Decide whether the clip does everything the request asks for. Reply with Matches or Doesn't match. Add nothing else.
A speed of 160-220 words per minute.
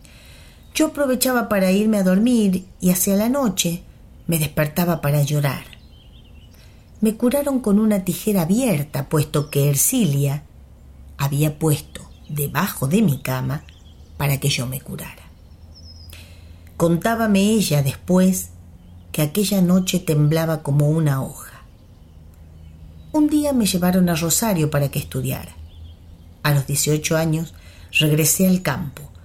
Doesn't match